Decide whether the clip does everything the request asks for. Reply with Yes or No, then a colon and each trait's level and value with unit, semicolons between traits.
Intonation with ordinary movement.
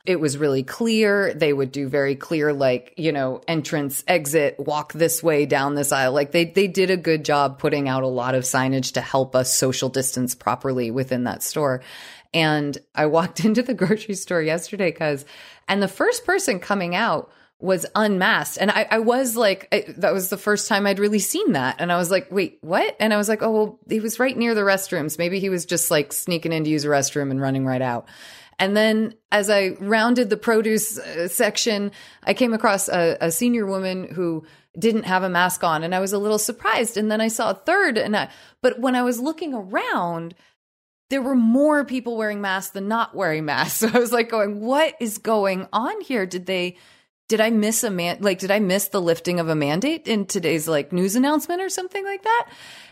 No: wide, 6.1 semitones